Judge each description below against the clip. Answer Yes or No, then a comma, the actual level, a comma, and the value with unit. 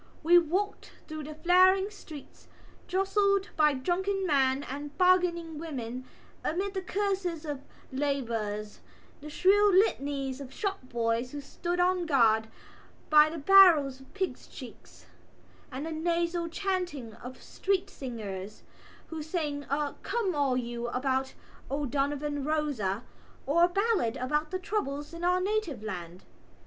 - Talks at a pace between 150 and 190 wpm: No, slow, 135 wpm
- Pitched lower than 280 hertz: No, very high, 300 Hz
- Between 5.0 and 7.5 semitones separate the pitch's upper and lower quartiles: Yes, wide, 5.6 semitones